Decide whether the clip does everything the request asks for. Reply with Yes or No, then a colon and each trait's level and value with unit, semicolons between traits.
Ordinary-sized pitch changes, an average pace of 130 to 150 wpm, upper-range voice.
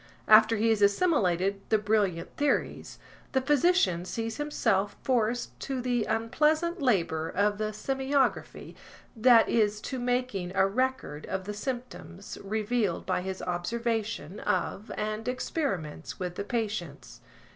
Yes: average, 4.4 semitones; slow, 135 wpm; high, 220 Hz